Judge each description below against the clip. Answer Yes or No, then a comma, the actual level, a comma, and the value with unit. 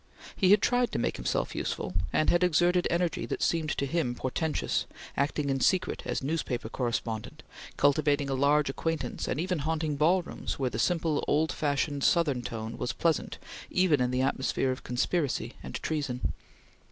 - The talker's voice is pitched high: No, medium, 145 Hz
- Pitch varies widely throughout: No, average, 4.1 semitones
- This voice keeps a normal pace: Yes, average, 165 wpm